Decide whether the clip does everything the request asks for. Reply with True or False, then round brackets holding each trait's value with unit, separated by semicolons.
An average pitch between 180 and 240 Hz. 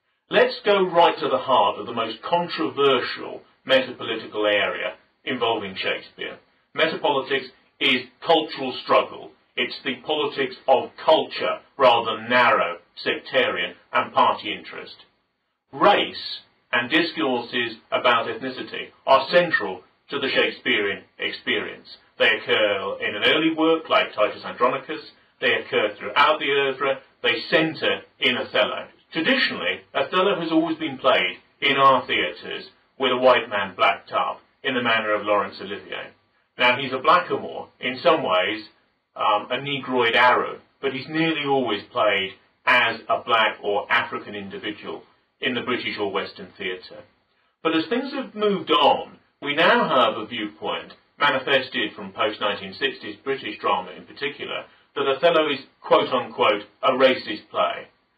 False (140 Hz)